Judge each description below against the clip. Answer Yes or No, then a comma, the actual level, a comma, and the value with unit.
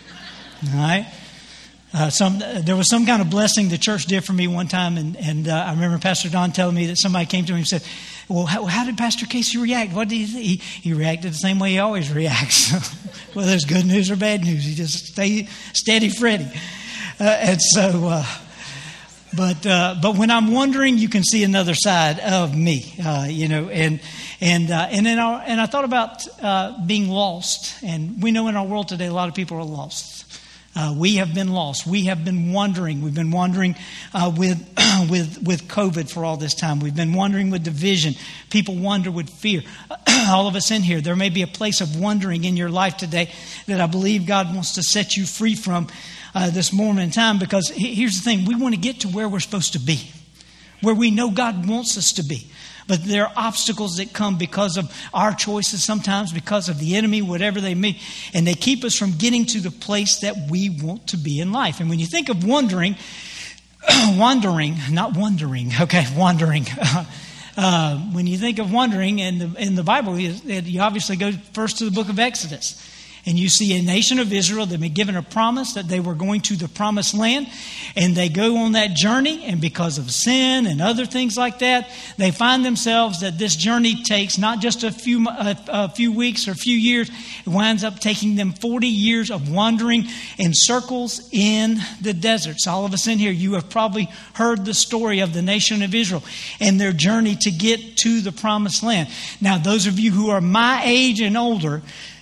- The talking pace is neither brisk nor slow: No, fast, 215 wpm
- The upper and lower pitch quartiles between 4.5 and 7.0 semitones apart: No, average, 3.8 semitones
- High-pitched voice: Yes, high, 195 Hz